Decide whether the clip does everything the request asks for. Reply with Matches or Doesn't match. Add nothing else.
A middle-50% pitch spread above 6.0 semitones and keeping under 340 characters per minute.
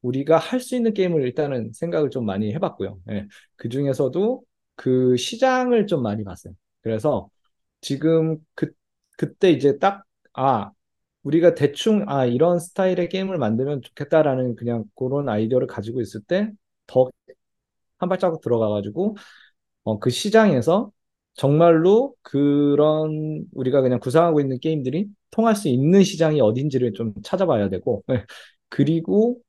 Matches